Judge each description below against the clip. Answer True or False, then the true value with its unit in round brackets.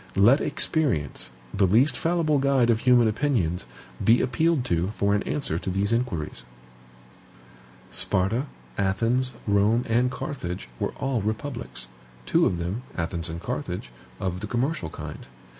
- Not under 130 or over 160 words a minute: True (140 wpm)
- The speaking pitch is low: True (110 Hz)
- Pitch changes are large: True (6.3 semitones)